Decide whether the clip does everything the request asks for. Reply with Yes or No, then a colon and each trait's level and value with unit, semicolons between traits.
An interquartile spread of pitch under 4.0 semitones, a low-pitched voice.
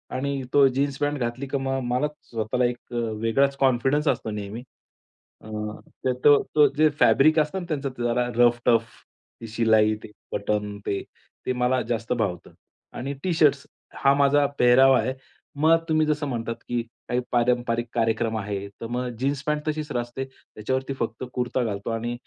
Yes: average, 3.3 semitones; low, 125 Hz